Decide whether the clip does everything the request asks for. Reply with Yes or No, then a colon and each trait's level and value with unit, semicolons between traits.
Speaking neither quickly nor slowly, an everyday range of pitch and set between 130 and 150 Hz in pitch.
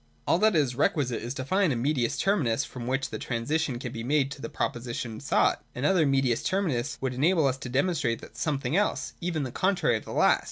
No: fast, 225 wpm; average, 4.7 semitones; low, 135 Hz